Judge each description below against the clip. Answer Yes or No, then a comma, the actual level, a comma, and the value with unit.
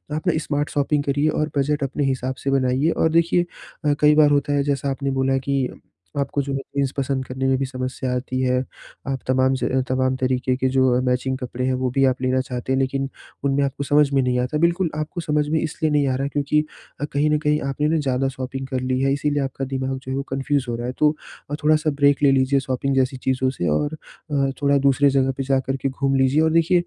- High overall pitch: No, low, 135 Hz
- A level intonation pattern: Yes, narrow, 1.8 semitones